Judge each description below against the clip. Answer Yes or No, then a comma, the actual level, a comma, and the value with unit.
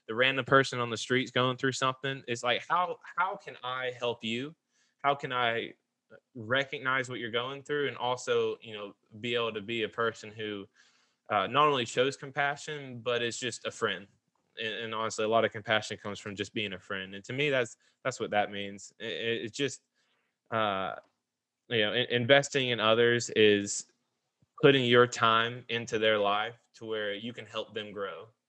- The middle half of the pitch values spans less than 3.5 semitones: Yes, average, 3.1 semitones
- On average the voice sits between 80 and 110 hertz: No, low, 120 Hz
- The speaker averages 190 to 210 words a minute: Yes, average, 195 wpm